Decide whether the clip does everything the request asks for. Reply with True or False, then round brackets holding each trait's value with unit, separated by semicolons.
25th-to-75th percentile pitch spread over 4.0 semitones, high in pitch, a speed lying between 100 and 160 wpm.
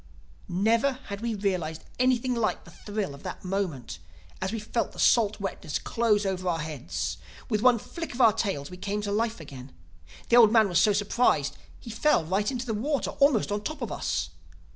False (5.3 semitones; 205 Hz; 205 wpm)